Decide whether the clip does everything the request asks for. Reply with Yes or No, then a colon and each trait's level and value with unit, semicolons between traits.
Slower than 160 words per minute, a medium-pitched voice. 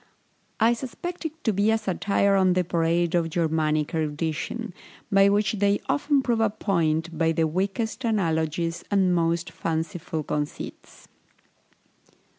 Yes: slow, 135 wpm; medium, 180 Hz